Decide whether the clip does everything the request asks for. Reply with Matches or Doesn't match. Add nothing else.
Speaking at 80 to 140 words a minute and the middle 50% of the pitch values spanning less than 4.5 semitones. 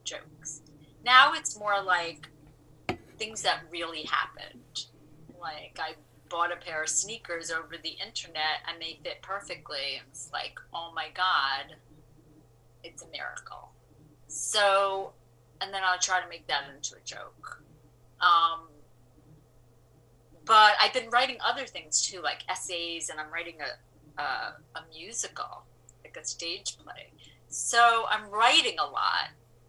Doesn't match